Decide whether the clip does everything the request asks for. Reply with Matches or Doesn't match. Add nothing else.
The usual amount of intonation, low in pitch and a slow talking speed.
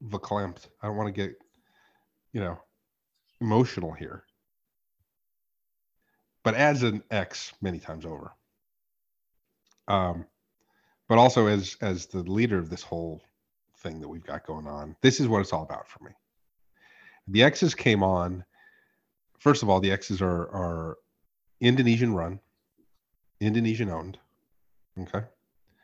Matches